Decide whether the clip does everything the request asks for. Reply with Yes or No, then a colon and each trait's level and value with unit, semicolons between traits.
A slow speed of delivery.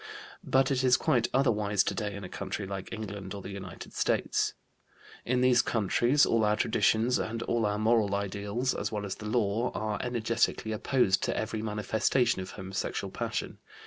No: average, 175 wpm